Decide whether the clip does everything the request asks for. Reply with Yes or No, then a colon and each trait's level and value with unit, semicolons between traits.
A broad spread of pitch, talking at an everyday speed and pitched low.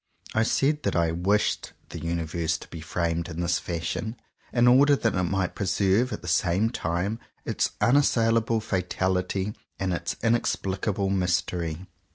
No: average, 4.7 semitones; average, 155 wpm; very low, 95 Hz